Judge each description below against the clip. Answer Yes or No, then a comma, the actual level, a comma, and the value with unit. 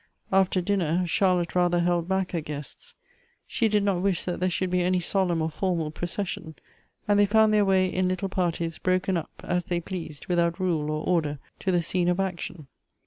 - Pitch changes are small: Yes, narrow, 1.9 semitones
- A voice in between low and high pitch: Yes, medium, 180 Hz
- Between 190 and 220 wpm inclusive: Yes, average, 195 wpm